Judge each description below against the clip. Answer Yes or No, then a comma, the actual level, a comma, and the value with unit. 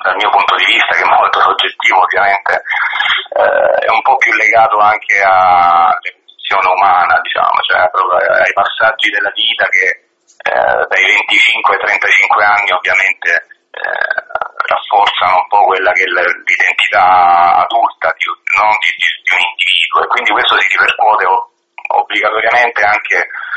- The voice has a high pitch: Yes, very high, 360 Hz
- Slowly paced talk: No, average, 135 wpm